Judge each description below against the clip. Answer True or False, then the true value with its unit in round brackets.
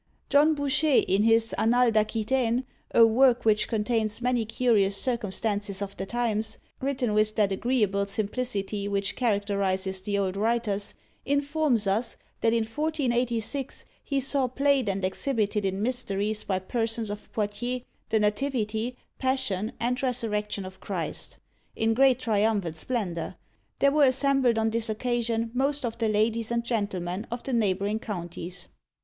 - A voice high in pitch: True (225 Hz)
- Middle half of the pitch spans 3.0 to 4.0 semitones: True (3.6 semitones)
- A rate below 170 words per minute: True (145 wpm)